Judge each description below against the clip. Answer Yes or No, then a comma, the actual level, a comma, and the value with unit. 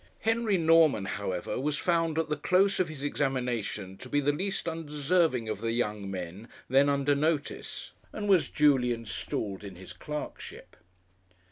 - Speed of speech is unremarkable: Yes, average, 155 wpm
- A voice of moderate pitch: Yes, medium, 145 Hz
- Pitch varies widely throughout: Yes, wide, 6.3 semitones